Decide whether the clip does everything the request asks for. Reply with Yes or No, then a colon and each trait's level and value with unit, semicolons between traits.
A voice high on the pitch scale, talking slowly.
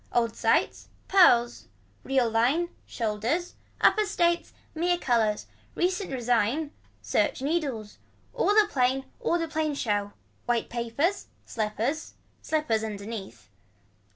Yes: very high, 255 Hz; slow, 110 wpm